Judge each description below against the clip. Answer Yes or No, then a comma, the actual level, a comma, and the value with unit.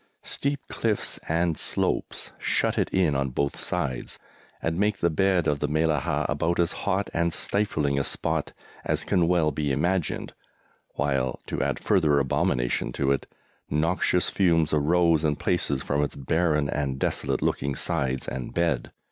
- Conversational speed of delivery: Yes, average, 155 wpm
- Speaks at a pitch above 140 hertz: No, very low, 80 Hz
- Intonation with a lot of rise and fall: No, average, 3.9 semitones